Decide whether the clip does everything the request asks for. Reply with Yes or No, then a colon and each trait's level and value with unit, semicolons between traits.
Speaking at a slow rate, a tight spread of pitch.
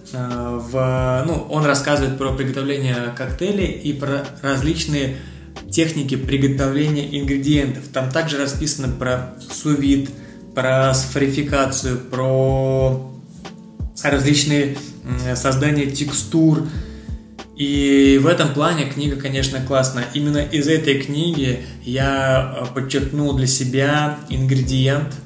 Yes: slow, 95 wpm; narrow, 1.8 semitones